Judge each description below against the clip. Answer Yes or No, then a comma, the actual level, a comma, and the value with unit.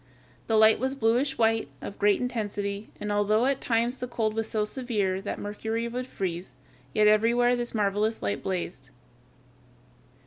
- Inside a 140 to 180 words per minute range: Yes, average, 160 wpm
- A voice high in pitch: Yes, high, 220 Hz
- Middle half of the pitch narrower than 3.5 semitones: Yes, average, 2.7 semitones